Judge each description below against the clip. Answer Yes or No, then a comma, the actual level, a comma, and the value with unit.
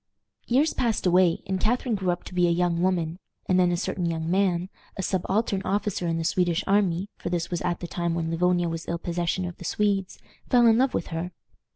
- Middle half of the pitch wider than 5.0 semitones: No, narrow, 2.4 semitones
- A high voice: No, medium, 180 Hz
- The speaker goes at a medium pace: No, fast, 225 wpm